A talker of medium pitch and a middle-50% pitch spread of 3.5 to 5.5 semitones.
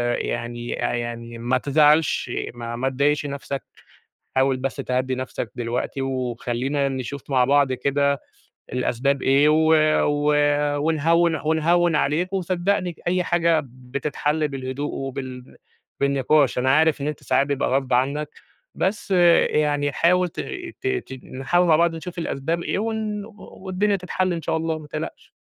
Yes: medium, 145 Hz; average, 3.9 semitones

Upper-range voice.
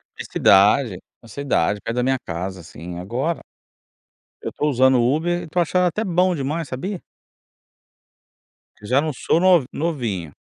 No: low, 135 Hz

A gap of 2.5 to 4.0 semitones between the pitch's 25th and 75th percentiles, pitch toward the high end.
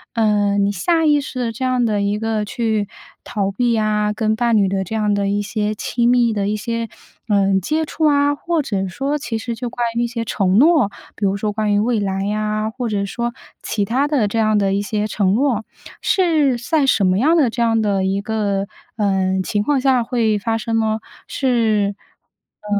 Yes: average, 3.1 semitones; high, 220 Hz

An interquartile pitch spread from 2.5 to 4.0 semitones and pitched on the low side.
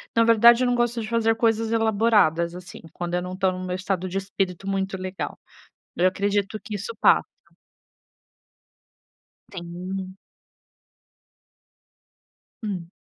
No: average, 3.4 semitones; high, 195 Hz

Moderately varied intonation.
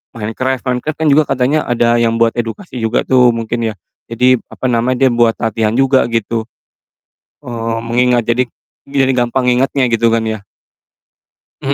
No: narrow, 2.0 semitones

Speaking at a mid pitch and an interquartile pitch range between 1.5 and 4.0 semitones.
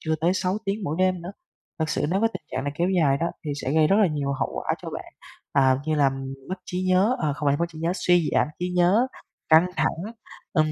Yes: medium, 170 Hz; average, 3.5 semitones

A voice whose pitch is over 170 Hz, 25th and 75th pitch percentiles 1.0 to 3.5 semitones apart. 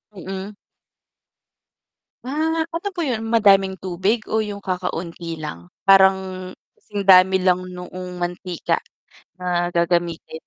Yes: medium, 185 Hz; narrow, 2.5 semitones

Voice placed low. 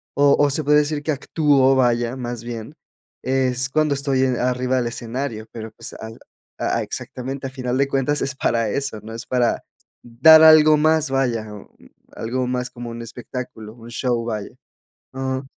Yes: low, 130 Hz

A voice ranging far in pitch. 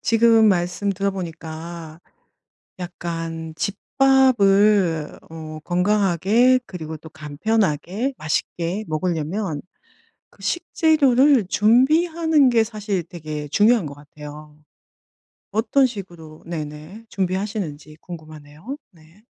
Yes: wide, 5.8 semitones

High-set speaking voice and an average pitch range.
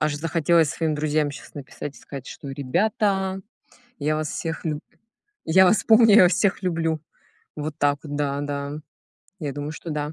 No: medium, 155 Hz; average, 3.1 semitones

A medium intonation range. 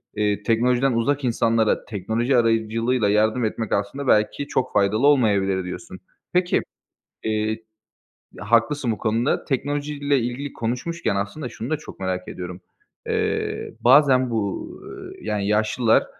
Yes: average, 3.9 semitones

